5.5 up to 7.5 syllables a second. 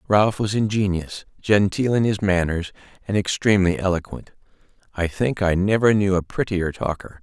No: 5.0 syllables/s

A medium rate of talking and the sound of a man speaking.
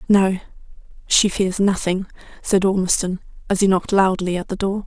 No: average, 160 wpm; female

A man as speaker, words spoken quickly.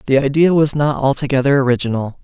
No: male; average, 160 wpm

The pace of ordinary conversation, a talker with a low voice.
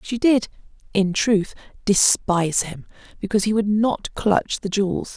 No: average, 150 wpm; high, 205 Hz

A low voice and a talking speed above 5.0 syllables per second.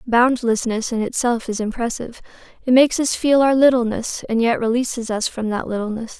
No: high, 235 Hz; 5.5 syllables/s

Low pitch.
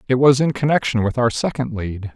Yes: low, 125 Hz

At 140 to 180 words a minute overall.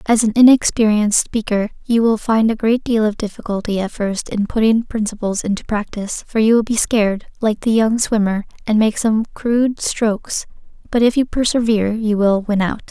No: average, 190 wpm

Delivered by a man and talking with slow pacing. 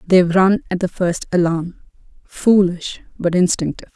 No: female; slow, 120 wpm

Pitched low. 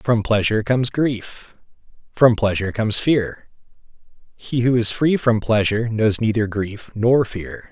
Yes: low, 110 Hz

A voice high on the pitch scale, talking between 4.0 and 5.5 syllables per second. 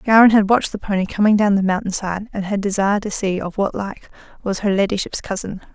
No: high, 200 Hz; 6.1 syllables/s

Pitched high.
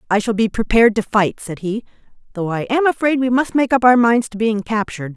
Yes: high, 225 Hz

